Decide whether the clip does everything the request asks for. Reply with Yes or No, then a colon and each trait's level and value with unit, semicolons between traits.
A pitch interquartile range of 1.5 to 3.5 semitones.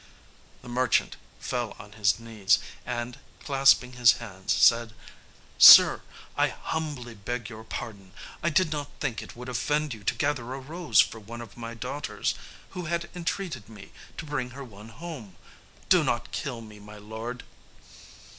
No: average, 4.4 semitones